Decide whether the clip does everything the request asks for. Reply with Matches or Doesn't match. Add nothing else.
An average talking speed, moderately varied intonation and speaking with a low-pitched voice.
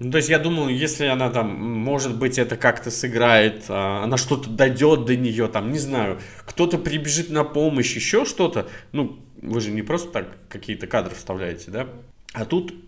Doesn't match